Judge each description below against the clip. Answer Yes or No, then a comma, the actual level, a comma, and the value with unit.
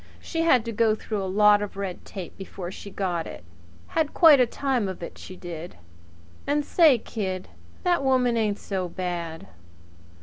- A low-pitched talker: No, high, 205 Hz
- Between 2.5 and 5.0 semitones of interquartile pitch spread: No, wide, 5.5 semitones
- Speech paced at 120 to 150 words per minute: No, average, 175 wpm